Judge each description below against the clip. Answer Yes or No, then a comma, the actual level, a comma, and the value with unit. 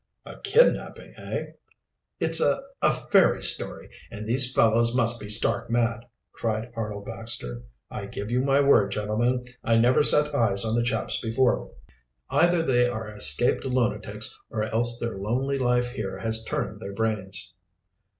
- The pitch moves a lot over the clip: No, narrow, 2.5 semitones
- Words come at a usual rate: Yes, average, 155 wpm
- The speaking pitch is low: Yes, low, 115 Hz